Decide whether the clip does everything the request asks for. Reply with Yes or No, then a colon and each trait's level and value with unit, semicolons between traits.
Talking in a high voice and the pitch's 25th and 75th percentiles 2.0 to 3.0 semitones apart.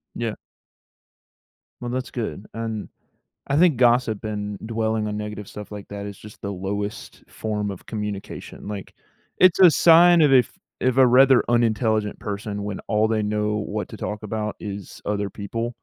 No: low, 105 Hz; narrow, 2.6 semitones